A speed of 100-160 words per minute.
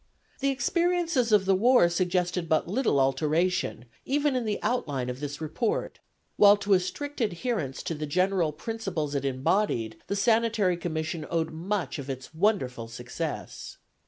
Yes: average, 155 wpm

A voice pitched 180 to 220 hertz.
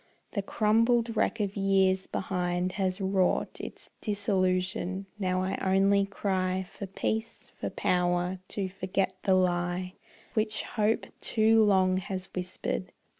Yes: high, 190 Hz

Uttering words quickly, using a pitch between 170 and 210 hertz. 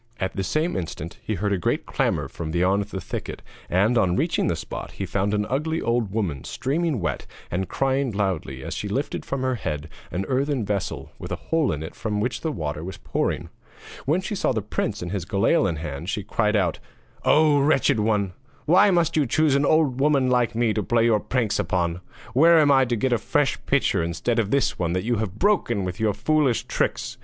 No: fast, 220 wpm; low, 110 Hz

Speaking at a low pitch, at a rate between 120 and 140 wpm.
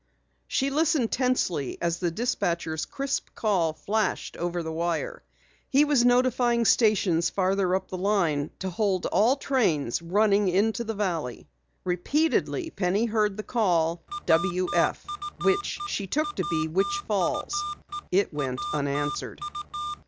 No: high, 195 Hz; slow, 135 wpm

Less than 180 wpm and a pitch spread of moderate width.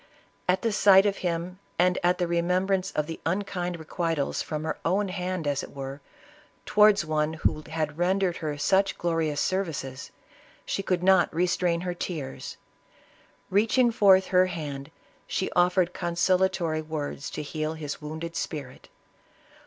Yes: average, 150 wpm; average, 3.2 semitones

